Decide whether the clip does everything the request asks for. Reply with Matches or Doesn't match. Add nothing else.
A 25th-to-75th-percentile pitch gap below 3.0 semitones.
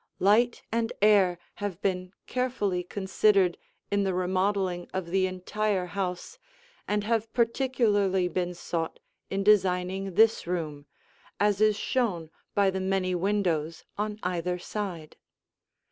Matches